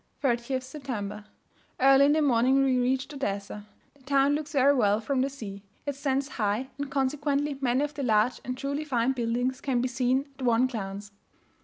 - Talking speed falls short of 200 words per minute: Yes, average, 185 wpm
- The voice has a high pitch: Yes, very high, 260 Hz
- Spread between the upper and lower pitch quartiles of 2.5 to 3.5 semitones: Yes, average, 2.8 semitones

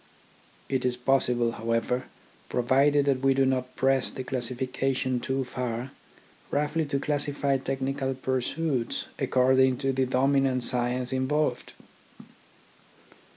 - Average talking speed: No, slow, 115 wpm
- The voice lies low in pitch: Yes, low, 130 Hz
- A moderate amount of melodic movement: No, narrow, 1.3 semitones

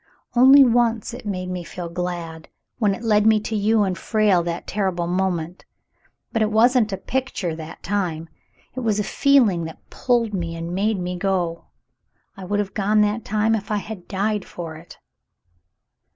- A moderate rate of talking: Yes, average, 180 wpm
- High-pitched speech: Yes, high, 200 Hz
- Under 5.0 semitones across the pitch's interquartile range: Yes, average, 3.7 semitones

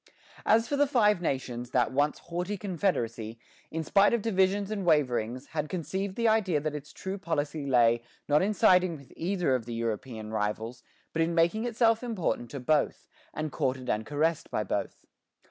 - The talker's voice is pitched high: No, medium, 160 Hz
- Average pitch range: No, wide, 7.4 semitones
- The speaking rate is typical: Yes, average, 180 wpm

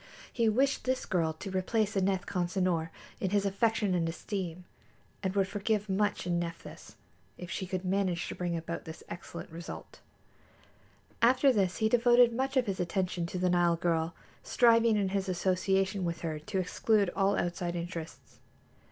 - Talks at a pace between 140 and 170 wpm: Yes, average, 165 wpm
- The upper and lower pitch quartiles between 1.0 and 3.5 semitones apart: Yes, average, 3.1 semitones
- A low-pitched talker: No, high, 190 Hz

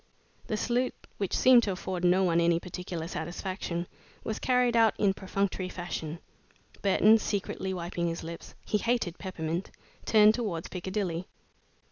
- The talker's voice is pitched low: No, medium, 185 Hz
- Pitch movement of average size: Yes, average, 3.6 semitones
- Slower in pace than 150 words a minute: Yes, average, 140 wpm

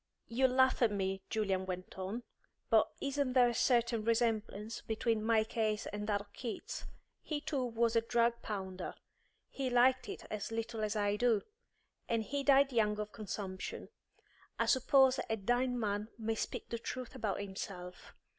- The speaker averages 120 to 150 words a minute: No, average, 165 wpm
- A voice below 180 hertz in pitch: No, high, 225 Hz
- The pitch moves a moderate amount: Yes, average, 3.0 semitones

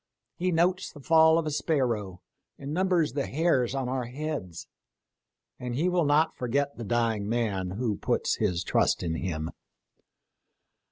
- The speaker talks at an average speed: Yes, average, 155 wpm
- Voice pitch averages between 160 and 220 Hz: No, low, 130 Hz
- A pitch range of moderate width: No, wide, 6.6 semitones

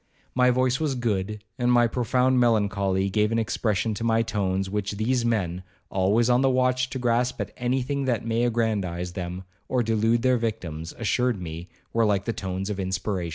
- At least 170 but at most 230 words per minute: Yes, average, 190 wpm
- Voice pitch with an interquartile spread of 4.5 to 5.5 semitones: No, average, 4.1 semitones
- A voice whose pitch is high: No, low, 115 Hz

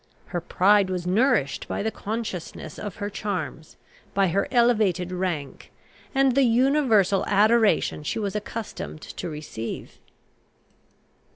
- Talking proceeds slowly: Yes, slow, 120 wpm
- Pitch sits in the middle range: No, high, 200 Hz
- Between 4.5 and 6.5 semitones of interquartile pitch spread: No, average, 4.1 semitones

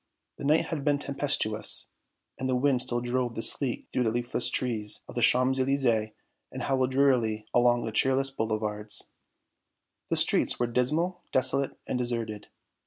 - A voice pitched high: No, low, 125 Hz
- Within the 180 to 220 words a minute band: No, average, 160 wpm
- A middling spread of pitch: Yes, average, 3.1 semitones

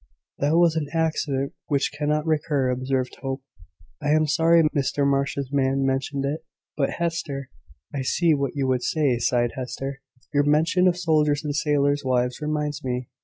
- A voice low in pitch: No, medium, 145 Hz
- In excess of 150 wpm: Yes, average, 170 wpm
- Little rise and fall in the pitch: Yes, narrow, 2.3 semitones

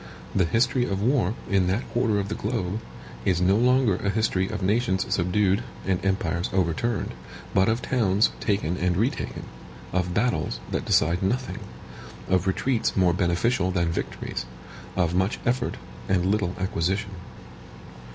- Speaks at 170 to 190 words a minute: No, average, 145 wpm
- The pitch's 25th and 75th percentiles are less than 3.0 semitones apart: No, average, 3.5 semitones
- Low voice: Yes, very low, 95 Hz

